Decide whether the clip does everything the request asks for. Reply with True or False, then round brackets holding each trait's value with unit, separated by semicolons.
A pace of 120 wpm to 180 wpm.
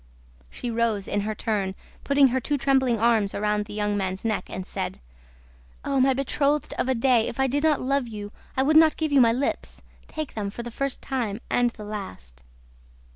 False (205 wpm)